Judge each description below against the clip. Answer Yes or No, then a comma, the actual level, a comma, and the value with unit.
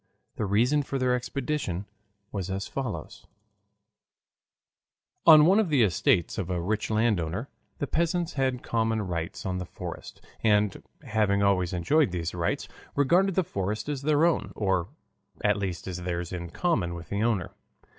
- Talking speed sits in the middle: Yes, average, 155 wpm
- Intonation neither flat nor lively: No, wide, 7.2 semitones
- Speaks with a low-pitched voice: Yes, low, 105 Hz